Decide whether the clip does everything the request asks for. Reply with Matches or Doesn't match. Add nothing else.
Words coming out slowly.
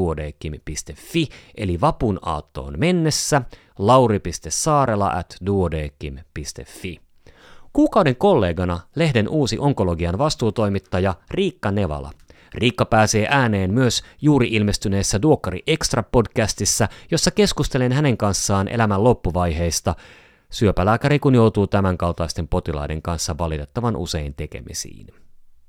Matches